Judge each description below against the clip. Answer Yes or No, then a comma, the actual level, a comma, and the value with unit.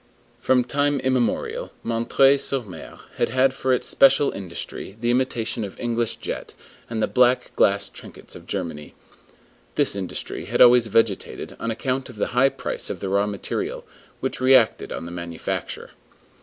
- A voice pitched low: Yes, low, 115 Hz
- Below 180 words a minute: Yes, average, 160 wpm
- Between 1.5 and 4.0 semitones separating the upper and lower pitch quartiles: No, average, 4.4 semitones